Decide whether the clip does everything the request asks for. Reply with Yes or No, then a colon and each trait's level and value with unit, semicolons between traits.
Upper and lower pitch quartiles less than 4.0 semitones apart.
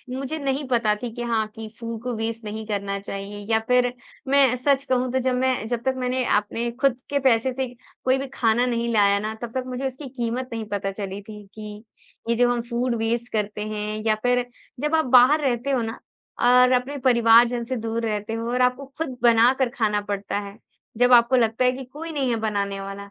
Yes: average, 2.8 semitones